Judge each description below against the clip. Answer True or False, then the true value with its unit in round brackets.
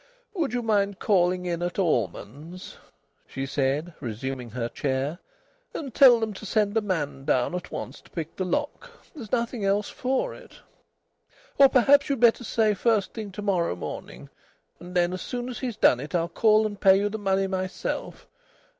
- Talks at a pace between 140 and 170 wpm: False (180 wpm)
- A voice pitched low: False (195 Hz)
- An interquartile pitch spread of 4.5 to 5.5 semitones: True (5.2 semitones)